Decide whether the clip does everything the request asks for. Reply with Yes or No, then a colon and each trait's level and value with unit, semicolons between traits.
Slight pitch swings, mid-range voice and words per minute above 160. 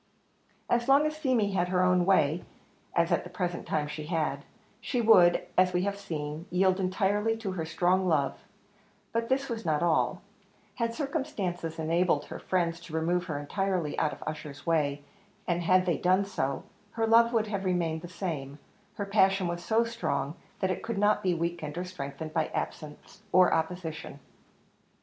No: average, 3.9 semitones; medium, 180 Hz; average, 175 wpm